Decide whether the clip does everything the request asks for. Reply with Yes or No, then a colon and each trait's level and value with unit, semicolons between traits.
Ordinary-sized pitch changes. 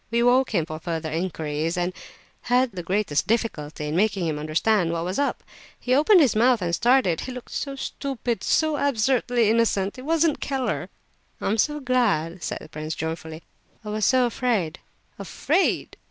No: wide, 7.4 semitones